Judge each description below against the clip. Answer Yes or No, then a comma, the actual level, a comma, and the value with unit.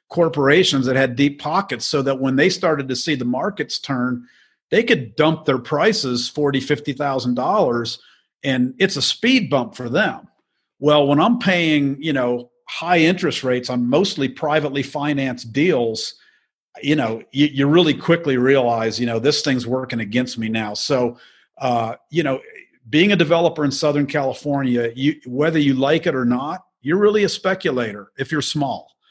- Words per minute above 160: Yes, average, 175 wpm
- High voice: No, medium, 140 Hz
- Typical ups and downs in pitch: Yes, average, 3.7 semitones